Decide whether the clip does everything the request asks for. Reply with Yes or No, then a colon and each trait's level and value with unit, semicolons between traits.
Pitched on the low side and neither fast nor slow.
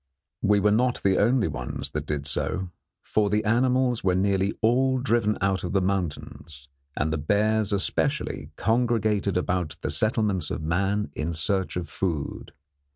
Yes: low, 100 Hz; average, 160 wpm